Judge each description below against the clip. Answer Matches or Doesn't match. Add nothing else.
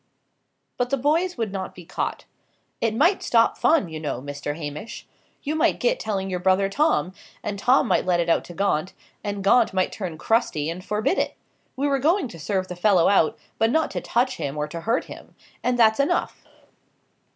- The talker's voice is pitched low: Doesn't match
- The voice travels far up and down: Matches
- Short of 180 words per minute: Doesn't match